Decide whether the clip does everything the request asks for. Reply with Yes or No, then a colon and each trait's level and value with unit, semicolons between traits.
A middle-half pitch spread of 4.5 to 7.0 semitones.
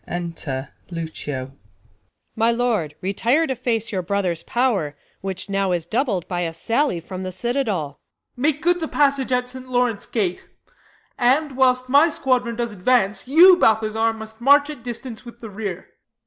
Yes: wide, 5.6 semitones